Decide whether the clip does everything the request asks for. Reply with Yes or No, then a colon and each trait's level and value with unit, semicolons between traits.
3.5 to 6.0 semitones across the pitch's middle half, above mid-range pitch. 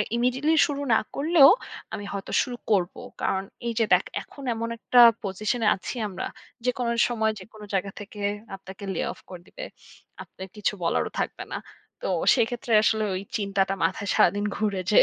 Yes: average, 3.8 semitones; high, 215 Hz